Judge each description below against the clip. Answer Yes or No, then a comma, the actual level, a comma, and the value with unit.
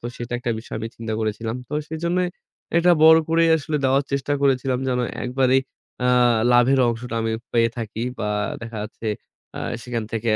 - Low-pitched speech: Yes, low, 125 Hz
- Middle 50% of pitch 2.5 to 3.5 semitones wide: Yes, average, 3.1 semitones